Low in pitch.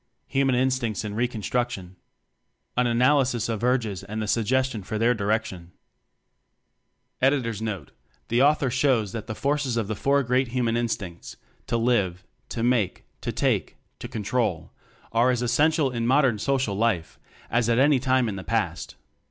Yes: low, 120 Hz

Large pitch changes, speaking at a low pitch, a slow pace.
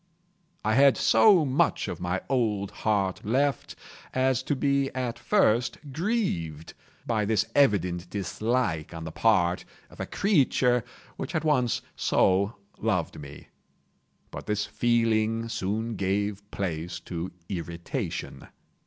Yes: wide, 5.7 semitones; low, 110 Hz; slow, 125 wpm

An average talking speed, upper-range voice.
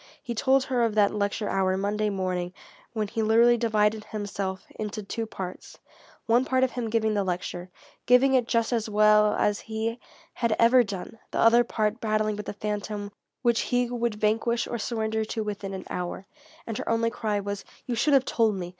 Yes: average, 195 wpm; high, 215 Hz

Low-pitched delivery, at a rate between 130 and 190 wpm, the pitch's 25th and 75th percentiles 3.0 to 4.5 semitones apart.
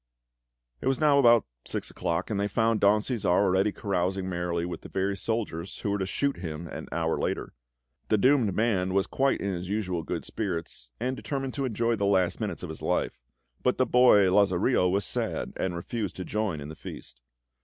No: low, 100 Hz; average, 200 wpm; average, 4.2 semitones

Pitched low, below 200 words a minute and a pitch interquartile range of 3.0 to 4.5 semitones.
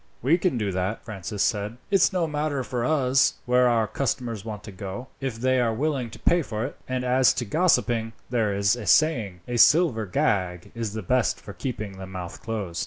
No: low, 115 Hz; fast, 205 wpm; average, 4.1 semitones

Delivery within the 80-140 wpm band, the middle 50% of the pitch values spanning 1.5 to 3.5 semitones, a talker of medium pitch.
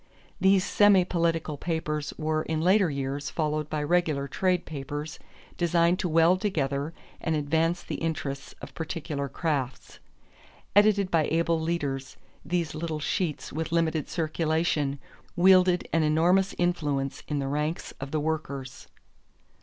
Yes: slow, 135 wpm; average, 2.9 semitones; medium, 160 Hz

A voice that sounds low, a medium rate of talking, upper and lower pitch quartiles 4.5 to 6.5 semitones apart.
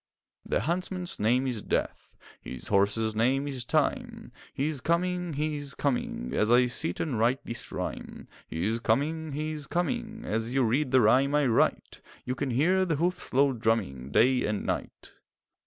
Yes: low, 130 Hz; average, 175 wpm; wide, 5.4 semitones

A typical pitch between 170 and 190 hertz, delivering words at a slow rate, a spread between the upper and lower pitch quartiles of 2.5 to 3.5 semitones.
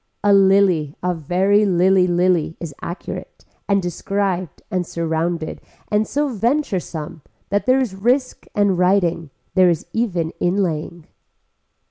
Yes: medium, 185 Hz; slow, 125 wpm; average, 3.1 semitones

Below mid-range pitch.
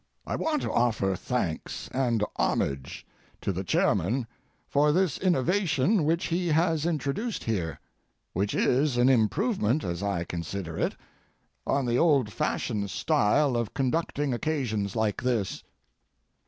Yes: low, 125 Hz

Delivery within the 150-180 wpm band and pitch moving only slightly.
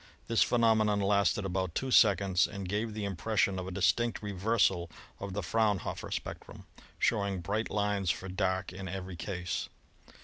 Yes: average, 165 wpm; narrow, 2.2 semitones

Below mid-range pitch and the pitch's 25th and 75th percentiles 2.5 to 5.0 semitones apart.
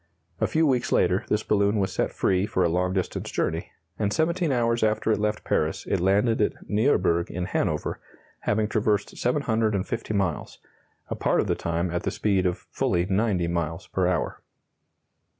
Yes: low, 100 Hz; average, 3.5 semitones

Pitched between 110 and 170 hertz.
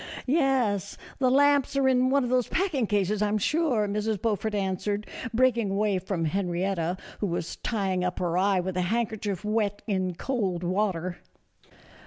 No: high, 205 Hz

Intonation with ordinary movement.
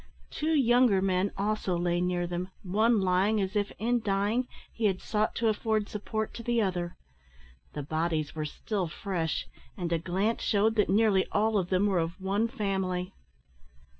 Yes: average, 3.3 semitones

